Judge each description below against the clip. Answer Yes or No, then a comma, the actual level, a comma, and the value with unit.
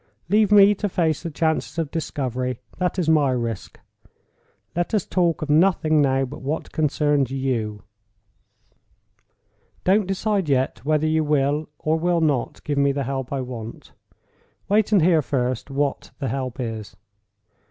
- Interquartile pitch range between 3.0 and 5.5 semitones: Yes, average, 4.1 semitones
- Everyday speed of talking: Yes, average, 150 wpm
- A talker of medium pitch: Yes, medium, 150 Hz